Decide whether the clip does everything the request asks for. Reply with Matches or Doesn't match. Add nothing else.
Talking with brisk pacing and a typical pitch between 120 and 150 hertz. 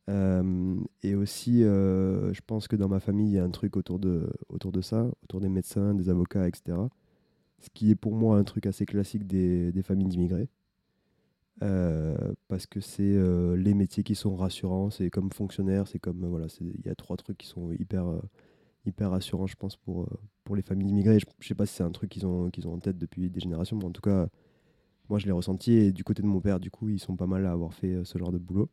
Doesn't match